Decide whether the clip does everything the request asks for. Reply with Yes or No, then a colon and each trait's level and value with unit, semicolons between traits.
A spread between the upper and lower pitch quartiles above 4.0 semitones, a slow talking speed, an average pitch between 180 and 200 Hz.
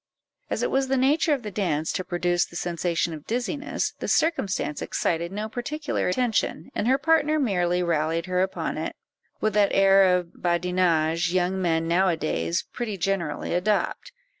No: average, 4.6 semitones; average, 170 wpm; medium, 185 Hz